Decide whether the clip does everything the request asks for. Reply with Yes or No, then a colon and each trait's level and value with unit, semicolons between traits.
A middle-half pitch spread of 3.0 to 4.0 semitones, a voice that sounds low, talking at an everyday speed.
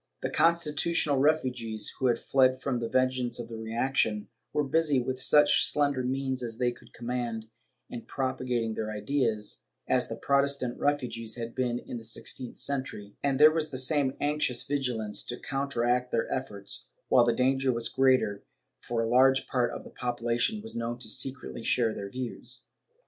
No: narrow, 2.6 semitones; low, 125 Hz; average, 175 wpm